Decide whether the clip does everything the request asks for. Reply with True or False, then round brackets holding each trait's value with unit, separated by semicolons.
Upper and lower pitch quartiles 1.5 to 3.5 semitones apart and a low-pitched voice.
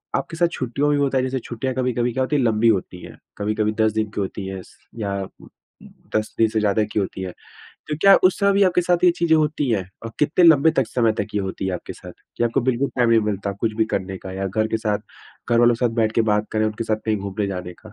False (4.1 semitones; 115 Hz)